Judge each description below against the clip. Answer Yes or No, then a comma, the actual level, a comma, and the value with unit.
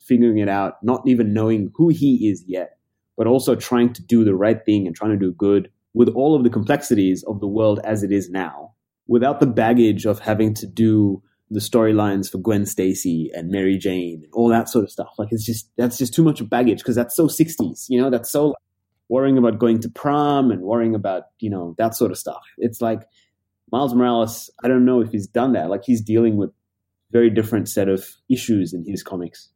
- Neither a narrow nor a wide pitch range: Yes, average, 3.2 semitones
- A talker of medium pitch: No, low, 110 Hz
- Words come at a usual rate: No, fast, 225 wpm